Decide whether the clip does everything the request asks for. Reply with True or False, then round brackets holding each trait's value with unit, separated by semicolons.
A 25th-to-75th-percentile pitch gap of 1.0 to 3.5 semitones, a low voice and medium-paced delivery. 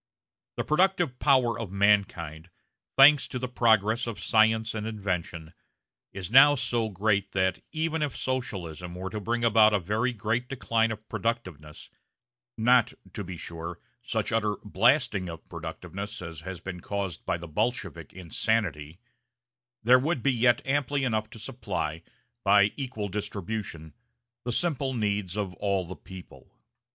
False (4.7 semitones; 105 Hz; 145 wpm)